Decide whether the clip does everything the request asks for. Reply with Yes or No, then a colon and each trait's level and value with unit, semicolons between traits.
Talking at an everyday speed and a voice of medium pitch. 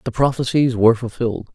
No: average, 155 wpm; low, 120 Hz